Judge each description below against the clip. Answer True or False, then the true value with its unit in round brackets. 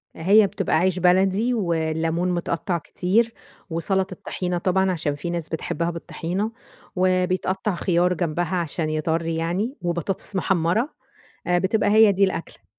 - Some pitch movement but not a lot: False (2.3 semitones)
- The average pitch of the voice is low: False (180 Hz)